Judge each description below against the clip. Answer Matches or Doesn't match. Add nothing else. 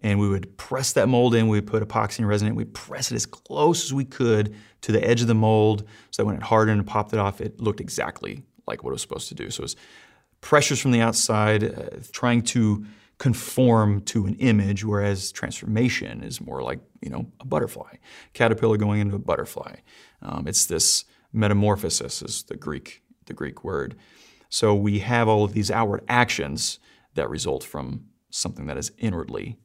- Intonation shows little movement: Matches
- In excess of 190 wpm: Matches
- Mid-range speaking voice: Doesn't match